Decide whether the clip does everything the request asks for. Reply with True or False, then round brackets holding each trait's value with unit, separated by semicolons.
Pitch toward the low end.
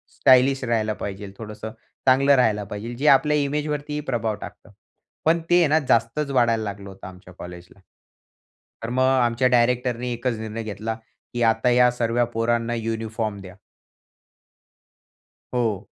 True (115 Hz)